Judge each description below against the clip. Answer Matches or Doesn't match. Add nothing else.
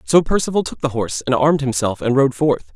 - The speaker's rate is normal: Doesn't match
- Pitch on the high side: Doesn't match